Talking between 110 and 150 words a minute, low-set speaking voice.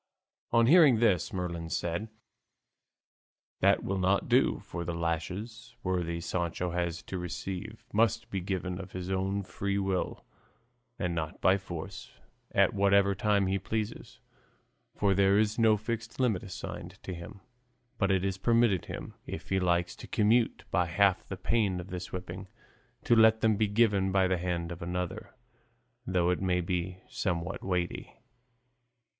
No: average, 160 wpm; very low, 95 Hz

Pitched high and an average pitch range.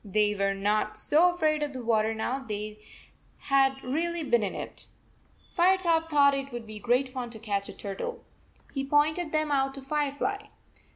No: very high, 270 Hz; wide, 6.0 semitones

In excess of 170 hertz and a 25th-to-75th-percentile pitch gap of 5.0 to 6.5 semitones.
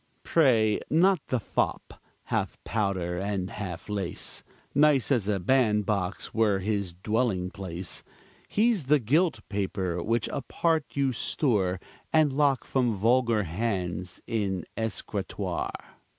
No: low, 105 Hz; wide, 5.6 semitones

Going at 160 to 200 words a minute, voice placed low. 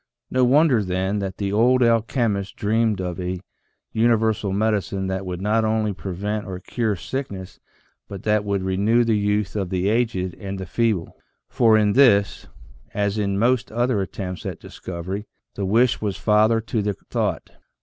Yes: average, 170 wpm; low, 105 Hz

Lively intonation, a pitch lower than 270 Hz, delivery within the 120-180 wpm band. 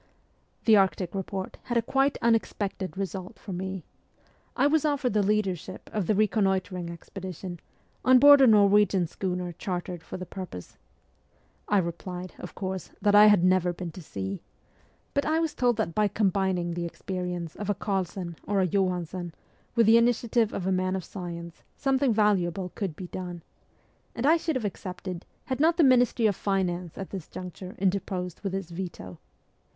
No: average, 3.0 semitones; high, 190 Hz; average, 175 wpm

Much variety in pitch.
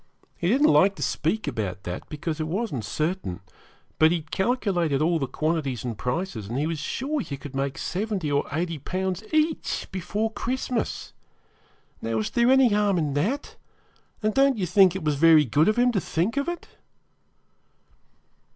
Yes: wide, 6.9 semitones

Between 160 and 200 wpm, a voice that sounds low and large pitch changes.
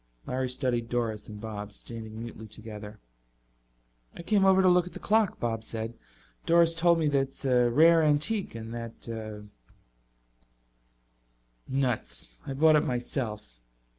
No: average, 145 wpm; low, 115 Hz; wide, 6.0 semitones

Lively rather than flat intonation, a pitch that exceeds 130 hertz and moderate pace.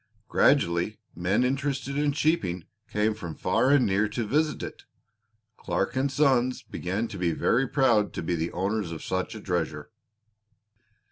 No: wide, 6.9 semitones; low, 110 Hz; average, 155 wpm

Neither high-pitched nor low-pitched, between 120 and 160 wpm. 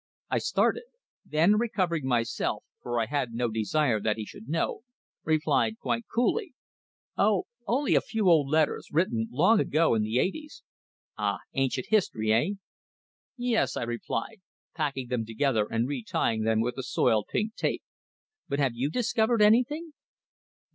Yes: medium, 145 Hz; average, 150 wpm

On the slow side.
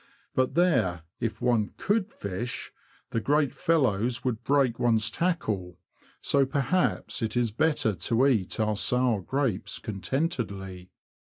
Yes: slow, 130 wpm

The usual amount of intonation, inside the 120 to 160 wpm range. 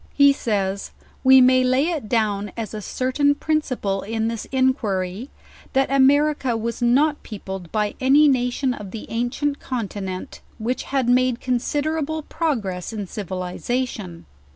Yes: average, 4.7 semitones; average, 140 wpm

